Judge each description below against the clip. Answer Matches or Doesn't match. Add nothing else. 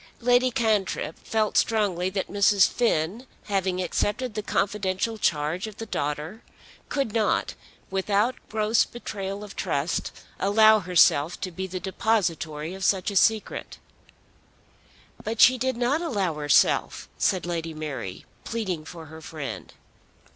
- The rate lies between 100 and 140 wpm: Matches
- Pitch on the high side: Matches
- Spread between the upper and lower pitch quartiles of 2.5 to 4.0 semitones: Doesn't match